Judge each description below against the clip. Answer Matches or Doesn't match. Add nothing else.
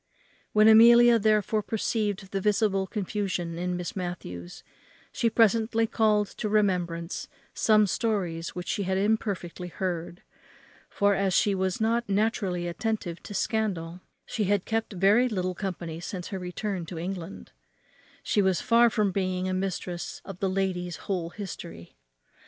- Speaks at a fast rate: Doesn't match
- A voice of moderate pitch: Doesn't match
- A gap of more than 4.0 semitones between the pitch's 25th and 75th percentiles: Doesn't match